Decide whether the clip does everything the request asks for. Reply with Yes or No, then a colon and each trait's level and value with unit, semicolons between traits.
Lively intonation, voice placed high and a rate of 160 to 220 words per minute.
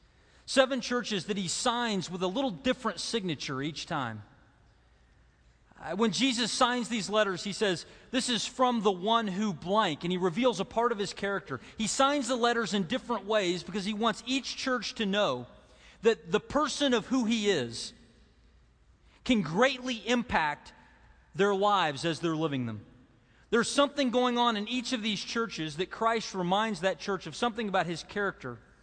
Yes: wide, 5.7 semitones; high, 210 Hz; average, 175 wpm